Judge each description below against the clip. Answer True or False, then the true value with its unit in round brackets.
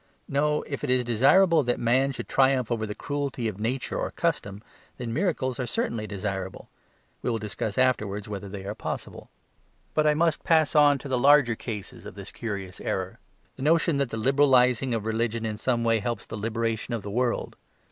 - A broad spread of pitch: False (4.1 semitones)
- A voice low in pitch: True (120 Hz)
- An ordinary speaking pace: True (195 wpm)